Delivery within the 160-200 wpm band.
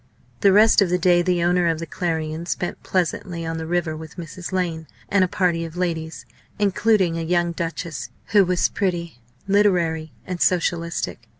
Yes: average, 175 wpm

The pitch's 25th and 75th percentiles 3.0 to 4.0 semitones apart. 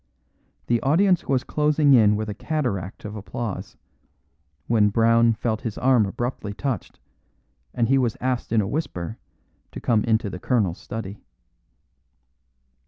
Yes: average, 3.7 semitones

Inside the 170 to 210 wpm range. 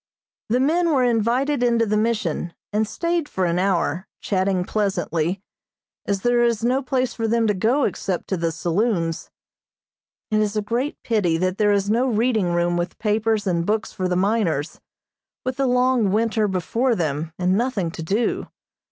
Yes: average, 175 wpm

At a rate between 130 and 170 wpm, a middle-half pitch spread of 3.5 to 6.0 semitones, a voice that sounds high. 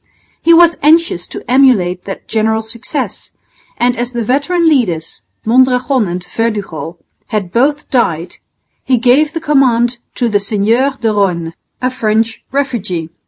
Yes: average, 140 wpm; average, 4.8 semitones; high, 235 Hz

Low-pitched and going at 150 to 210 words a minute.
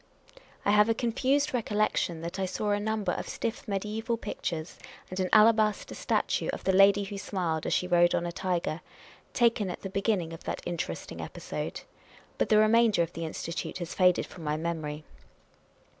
No: high, 195 Hz; average, 185 wpm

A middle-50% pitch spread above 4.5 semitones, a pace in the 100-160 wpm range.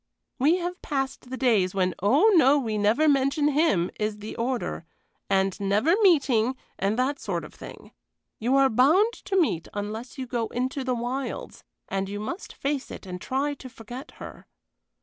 No: average, 5.2 semitones; average, 175 wpm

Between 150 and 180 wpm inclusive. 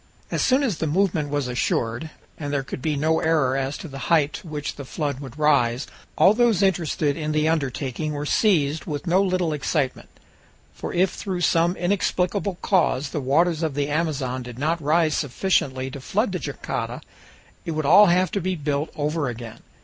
No: average, 190 wpm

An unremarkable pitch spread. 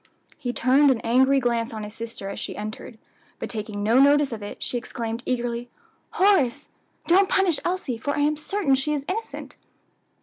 Yes: average, 4.3 semitones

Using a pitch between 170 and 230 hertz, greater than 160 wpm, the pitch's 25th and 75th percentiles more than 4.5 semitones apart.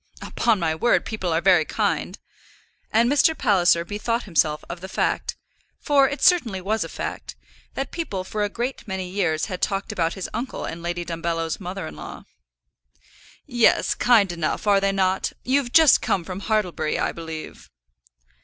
Yes: high, 190 Hz; average, 170 wpm; average, 5.1 semitones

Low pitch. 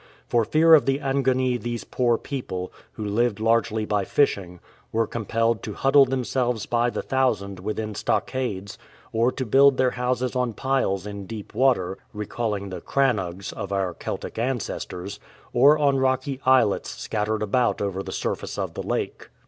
Yes: low, 115 Hz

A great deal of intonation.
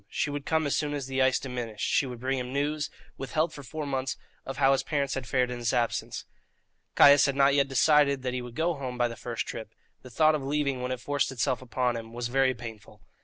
No: narrow, 2.5 semitones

